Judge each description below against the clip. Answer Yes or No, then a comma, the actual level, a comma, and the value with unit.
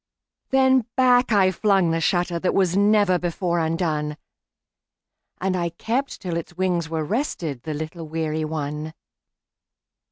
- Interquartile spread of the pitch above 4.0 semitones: No, average, 3.7 semitones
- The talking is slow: Yes, slow, 120 wpm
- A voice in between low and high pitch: Yes, medium, 175 Hz